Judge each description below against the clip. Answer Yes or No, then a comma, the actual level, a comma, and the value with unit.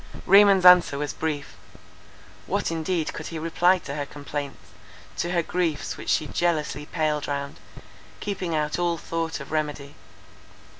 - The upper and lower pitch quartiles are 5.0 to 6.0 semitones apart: No, average, 3.0 semitones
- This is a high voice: No, medium, 160 Hz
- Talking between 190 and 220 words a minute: No, average, 145 wpm